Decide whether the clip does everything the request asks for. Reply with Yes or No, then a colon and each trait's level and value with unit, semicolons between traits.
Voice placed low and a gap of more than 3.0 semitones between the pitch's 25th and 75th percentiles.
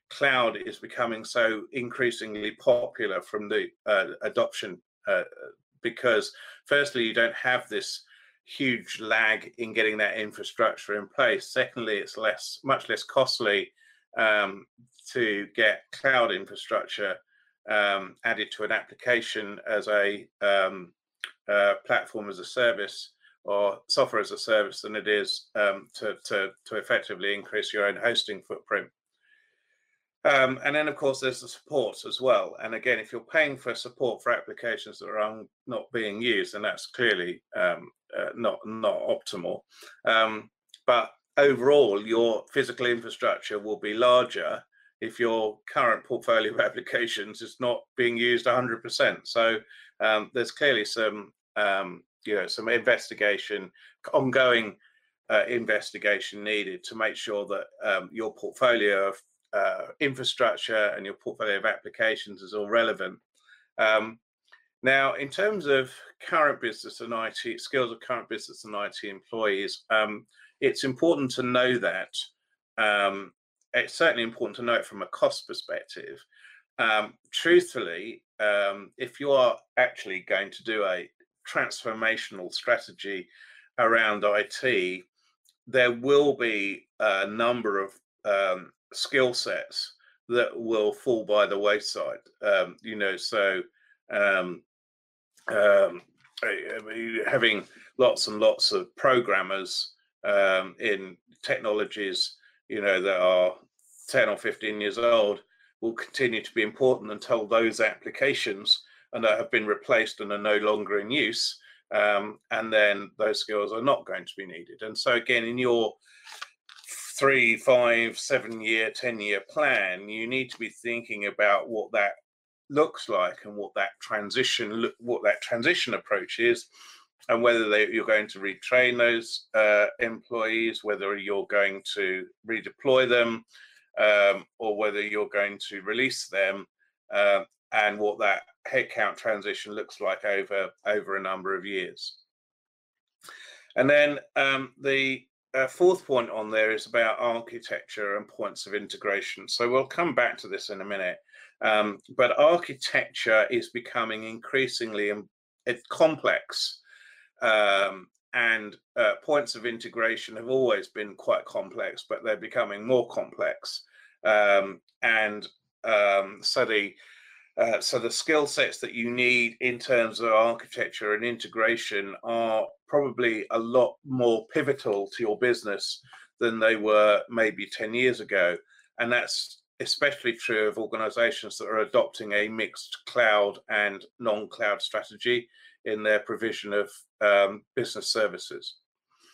Yes: low, 115 Hz; average, 4.5 semitones